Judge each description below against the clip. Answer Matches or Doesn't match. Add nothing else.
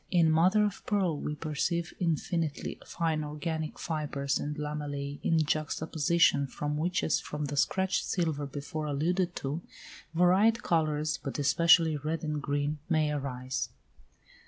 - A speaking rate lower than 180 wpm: Matches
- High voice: Doesn't match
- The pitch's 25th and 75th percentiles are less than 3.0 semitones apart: Matches